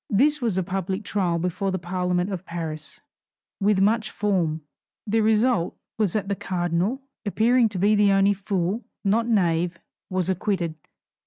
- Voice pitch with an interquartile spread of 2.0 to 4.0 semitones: Yes, average, 3.1 semitones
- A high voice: Yes, high, 195 Hz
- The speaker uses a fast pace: No, average, 150 wpm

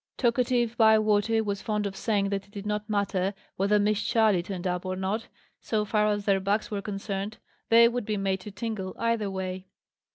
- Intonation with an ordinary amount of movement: No, narrow, 2.0 semitones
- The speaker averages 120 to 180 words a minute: No, average, 195 wpm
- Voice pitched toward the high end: Yes, high, 205 Hz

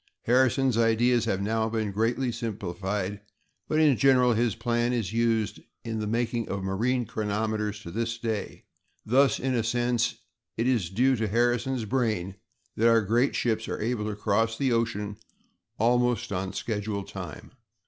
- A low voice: Yes, low, 115 Hz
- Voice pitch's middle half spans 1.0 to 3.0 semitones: Yes, narrow, 2.5 semitones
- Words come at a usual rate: Yes, average, 160 wpm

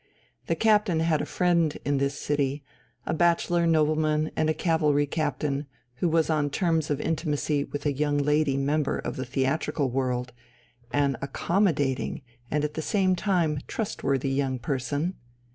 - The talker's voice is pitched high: No, medium, 150 Hz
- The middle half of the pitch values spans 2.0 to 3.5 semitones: Yes, average, 2.8 semitones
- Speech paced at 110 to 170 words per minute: Yes, average, 155 wpm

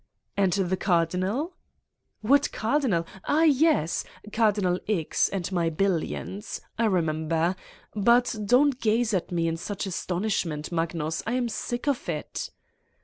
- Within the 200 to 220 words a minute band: No, average, 140 wpm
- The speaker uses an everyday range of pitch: No, wide, 5.9 semitones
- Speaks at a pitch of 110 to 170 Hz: No, high, 195 Hz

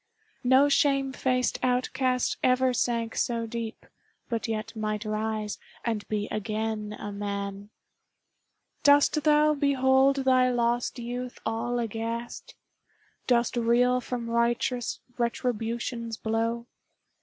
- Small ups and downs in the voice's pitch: Yes, narrow, 2.2 semitones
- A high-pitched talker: Yes, high, 235 Hz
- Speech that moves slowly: Yes, slow, 110 wpm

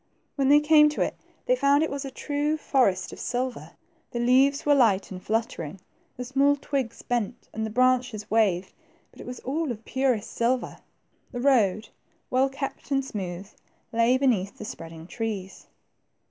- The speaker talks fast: No, average, 170 wpm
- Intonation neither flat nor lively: Yes, average, 4.5 semitones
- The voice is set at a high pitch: Yes, very high, 250 Hz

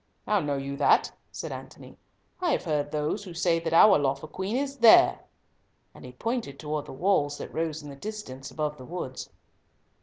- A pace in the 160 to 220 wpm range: Yes, average, 190 wpm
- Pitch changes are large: Yes, wide, 5.7 semitones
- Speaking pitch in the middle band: Yes, medium, 155 Hz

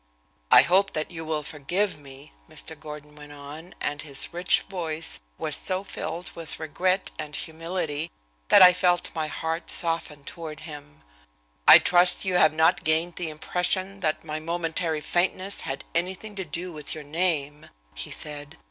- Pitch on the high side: No, medium, 160 Hz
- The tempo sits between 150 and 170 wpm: Yes, average, 165 wpm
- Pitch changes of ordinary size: Yes, average, 3.0 semitones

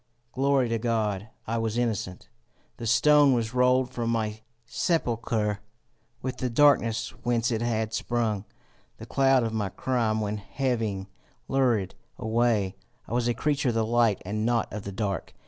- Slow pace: No, average, 160 wpm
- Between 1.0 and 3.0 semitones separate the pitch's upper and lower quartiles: Yes, narrow, 2.4 semitones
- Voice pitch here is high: No, low, 115 Hz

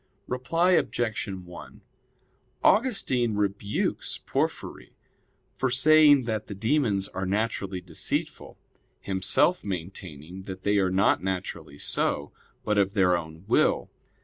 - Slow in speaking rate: Yes, slow, 115 wpm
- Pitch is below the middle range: Yes, low, 100 Hz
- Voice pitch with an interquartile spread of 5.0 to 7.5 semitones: No, average, 4.6 semitones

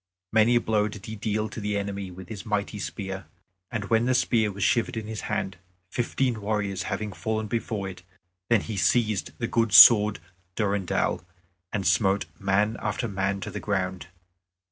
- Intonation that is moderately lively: No, narrow, 2.1 semitones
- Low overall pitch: Yes, low, 105 Hz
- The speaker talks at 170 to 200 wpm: Yes, average, 175 wpm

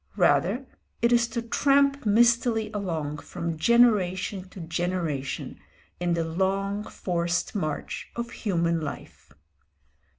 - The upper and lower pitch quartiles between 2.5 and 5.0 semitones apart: No, wide, 5.5 semitones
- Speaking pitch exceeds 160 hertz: Yes, high, 190 Hz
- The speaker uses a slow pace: Yes, slow, 110 wpm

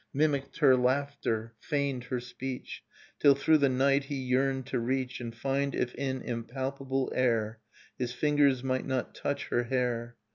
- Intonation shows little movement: Yes, narrow, 2.0 semitones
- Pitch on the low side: Yes, low, 130 Hz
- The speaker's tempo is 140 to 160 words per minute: Yes, average, 155 wpm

